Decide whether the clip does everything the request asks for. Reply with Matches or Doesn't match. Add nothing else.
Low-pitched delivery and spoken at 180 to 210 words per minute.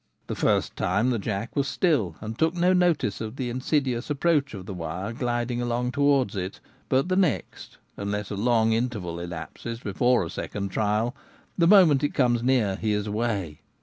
Matches